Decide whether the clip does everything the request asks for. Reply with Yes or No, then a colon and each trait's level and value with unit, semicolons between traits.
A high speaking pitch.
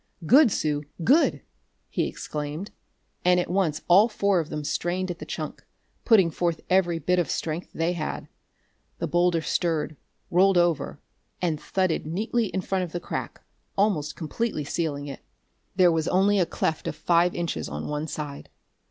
No: medium, 175 Hz